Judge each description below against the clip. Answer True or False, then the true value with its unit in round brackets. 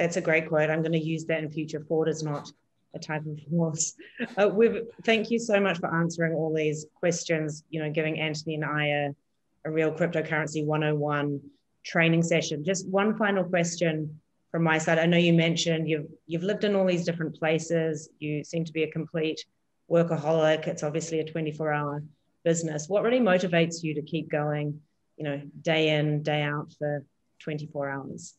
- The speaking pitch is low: False (160 Hz)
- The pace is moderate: True (185 wpm)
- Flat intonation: True (1.7 semitones)